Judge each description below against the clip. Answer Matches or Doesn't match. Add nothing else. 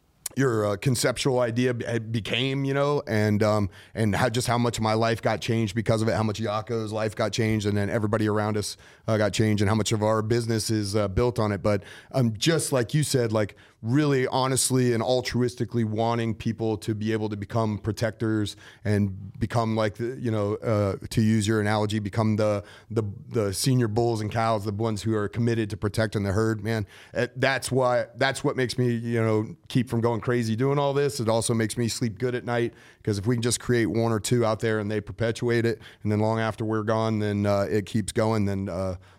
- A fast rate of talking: Matches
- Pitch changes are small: Matches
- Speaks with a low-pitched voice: Matches